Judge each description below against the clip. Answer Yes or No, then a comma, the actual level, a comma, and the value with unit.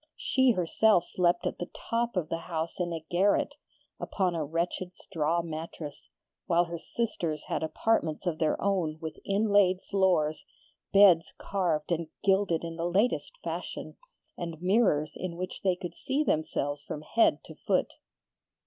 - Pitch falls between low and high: Yes, medium, 175 Hz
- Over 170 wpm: No, average, 155 wpm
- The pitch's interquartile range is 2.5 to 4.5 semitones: Yes, average, 3.4 semitones